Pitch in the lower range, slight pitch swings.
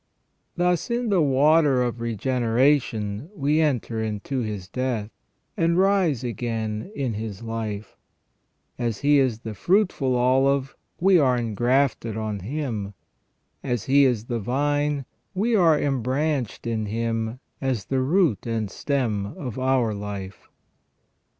No: low, 125 Hz; average, 4.5 semitones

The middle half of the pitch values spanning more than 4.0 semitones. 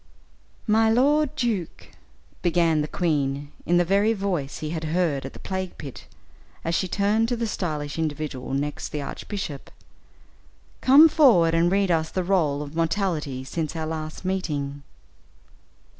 Yes: average, 5.0 semitones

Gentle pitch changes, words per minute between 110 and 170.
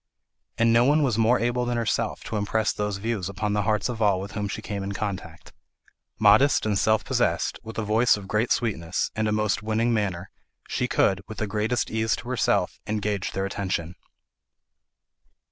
No: narrow, 2.2 semitones; average, 190 wpm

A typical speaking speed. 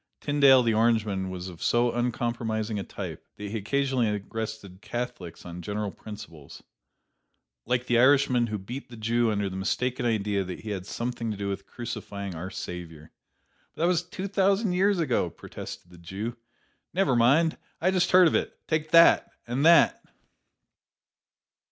Yes: average, 165 wpm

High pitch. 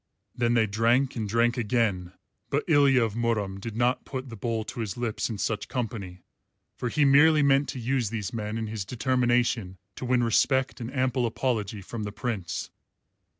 No: low, 115 Hz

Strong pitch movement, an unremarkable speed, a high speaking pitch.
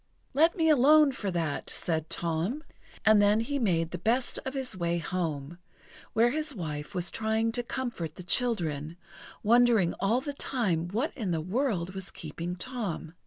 Yes: wide, 6.6 semitones; average, 165 wpm; high, 205 Hz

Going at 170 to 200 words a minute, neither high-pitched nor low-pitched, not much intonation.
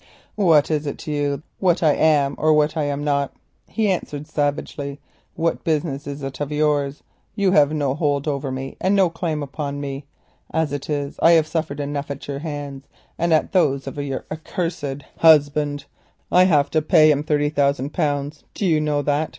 Yes: average, 195 wpm; medium, 145 Hz; narrow, 1.8 semitones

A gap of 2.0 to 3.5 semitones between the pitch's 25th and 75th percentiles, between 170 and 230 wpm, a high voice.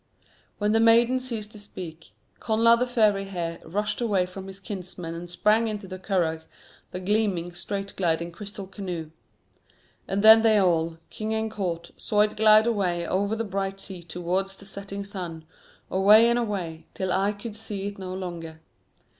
Yes: average, 3.2 semitones; average, 175 wpm; high, 195 Hz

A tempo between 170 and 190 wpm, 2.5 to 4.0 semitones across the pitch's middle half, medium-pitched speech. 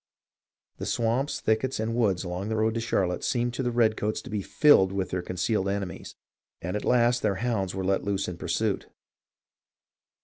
No: average, 180 wpm; average, 3.7 semitones; low, 105 Hz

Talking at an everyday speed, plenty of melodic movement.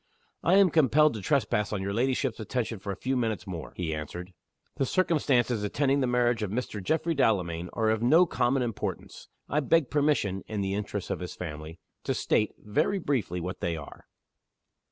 Yes: average, 185 wpm; wide, 6.1 semitones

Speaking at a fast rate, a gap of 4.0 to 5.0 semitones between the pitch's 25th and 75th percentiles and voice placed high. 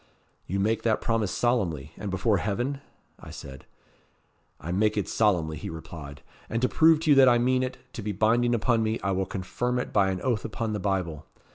No: fast, 210 wpm; average, 4.5 semitones; low, 105 Hz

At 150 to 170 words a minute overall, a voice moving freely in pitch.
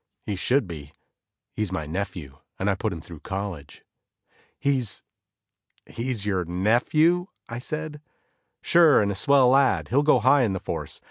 Yes: average, 155 wpm; wide, 6.8 semitones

